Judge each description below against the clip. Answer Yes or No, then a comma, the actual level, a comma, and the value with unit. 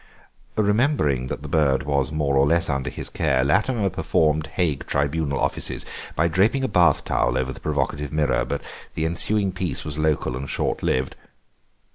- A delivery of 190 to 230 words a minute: No, average, 170 wpm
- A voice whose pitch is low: Yes, very low, 75 Hz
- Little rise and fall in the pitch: No, average, 4.5 semitones